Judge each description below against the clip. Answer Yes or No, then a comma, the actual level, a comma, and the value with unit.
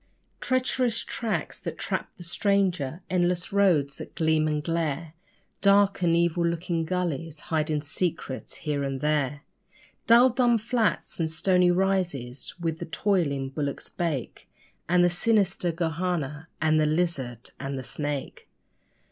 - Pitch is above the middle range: No, medium, 165 Hz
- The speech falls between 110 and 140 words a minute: Yes, slow, 135 wpm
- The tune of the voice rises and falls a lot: No, average, 3.6 semitones